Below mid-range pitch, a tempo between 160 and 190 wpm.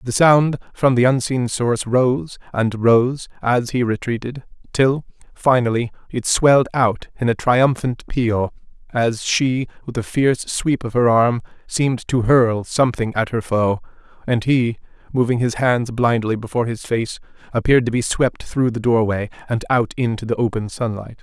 Yes: low, 120 Hz; average, 165 wpm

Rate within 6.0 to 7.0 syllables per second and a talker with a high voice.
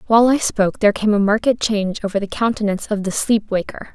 Yes: 6.7 syllables/s; high, 210 Hz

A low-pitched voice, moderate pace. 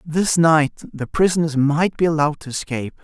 No: medium, 155 Hz; average, 180 wpm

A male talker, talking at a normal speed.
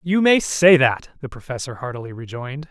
Yes: male; average, 180 wpm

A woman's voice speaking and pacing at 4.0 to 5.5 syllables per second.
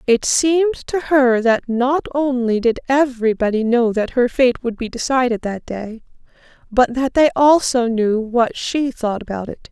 Yes: female; 4.4 syllables/s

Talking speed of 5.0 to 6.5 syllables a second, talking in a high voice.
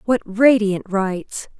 No: 3.6 syllables/s; high, 210 Hz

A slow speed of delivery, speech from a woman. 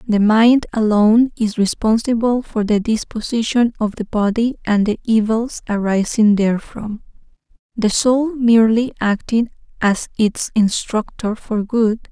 Yes: slow, 125 wpm; female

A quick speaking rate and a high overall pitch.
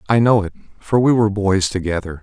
No: fast, 215 wpm; low, 100 Hz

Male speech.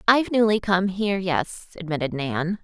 No: female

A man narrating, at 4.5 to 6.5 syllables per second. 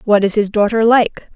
No: female; 5.0 syllables/s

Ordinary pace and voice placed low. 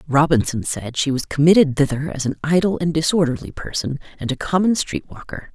No: average, 185 wpm; medium, 150 Hz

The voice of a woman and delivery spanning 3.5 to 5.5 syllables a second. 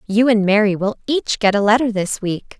Yes: female; 5.1 syllables/s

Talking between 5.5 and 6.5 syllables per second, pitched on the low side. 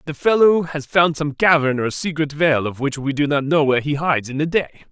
No: 5.7 syllables/s; medium, 150 Hz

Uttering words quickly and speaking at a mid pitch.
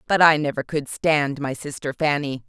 No: average, 195 wpm; medium, 145 Hz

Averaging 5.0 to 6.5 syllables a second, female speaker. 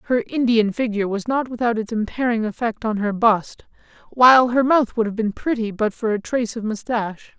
No: 5.5 syllables/s; male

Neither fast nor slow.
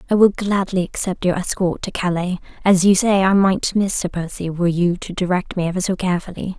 No: fast, 220 wpm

